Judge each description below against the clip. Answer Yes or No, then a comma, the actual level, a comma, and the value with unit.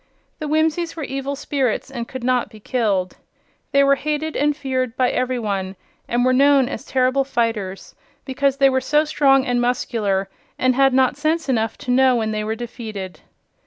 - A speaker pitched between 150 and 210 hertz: No, very high, 255 Hz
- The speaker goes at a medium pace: Yes, average, 185 wpm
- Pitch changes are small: No, average, 3.3 semitones